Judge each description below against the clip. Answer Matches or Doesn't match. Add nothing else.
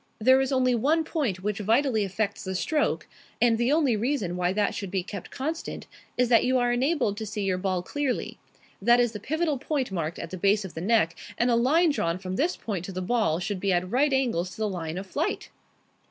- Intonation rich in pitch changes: Matches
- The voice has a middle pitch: Doesn't match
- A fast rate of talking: Matches